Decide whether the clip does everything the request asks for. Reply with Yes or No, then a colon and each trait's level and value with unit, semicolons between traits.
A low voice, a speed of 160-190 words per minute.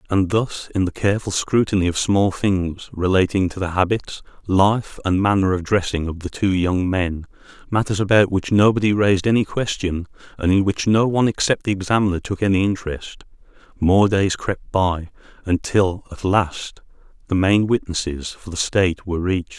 Yes: very low, 95 Hz; average, 165 wpm